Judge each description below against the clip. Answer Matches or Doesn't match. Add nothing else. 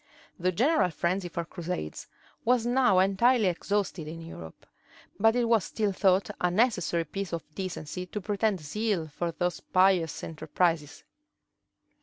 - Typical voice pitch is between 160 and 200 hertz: Matches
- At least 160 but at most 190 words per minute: Doesn't match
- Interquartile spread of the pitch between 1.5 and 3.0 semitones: Doesn't match